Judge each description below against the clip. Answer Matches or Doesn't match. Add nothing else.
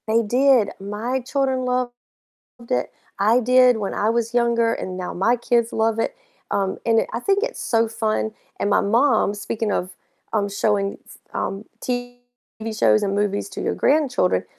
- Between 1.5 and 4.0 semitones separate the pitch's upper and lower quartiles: Matches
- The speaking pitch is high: Matches